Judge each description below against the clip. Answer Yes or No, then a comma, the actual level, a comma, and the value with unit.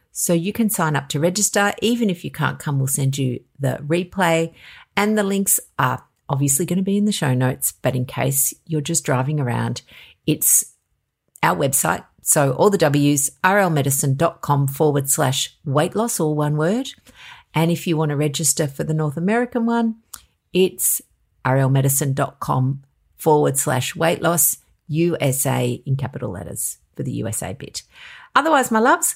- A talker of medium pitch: Yes, medium, 155 Hz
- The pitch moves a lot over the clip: Yes, wide, 5.9 semitones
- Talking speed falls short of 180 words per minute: Yes, average, 165 wpm